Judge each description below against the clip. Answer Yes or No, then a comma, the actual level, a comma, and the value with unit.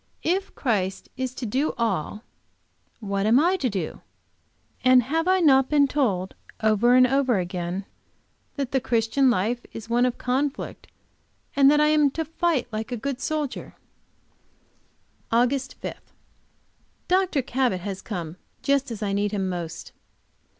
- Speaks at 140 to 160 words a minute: Yes, average, 150 wpm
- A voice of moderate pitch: No, very high, 250 Hz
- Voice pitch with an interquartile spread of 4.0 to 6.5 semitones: Yes, average, 5.2 semitones